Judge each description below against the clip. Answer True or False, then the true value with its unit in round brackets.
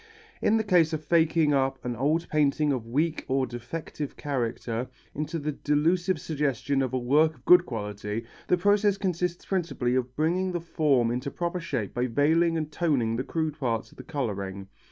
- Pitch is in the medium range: True (150 Hz)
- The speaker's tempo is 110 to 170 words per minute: False (180 wpm)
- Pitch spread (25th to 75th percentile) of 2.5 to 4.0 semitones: False (5.1 semitones)